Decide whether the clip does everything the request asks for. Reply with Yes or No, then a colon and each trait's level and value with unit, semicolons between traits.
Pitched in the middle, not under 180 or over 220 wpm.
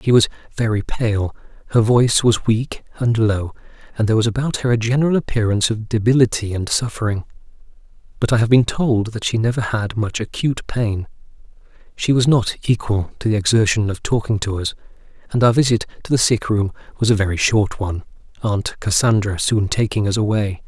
No: low, 110 Hz; average, 185 wpm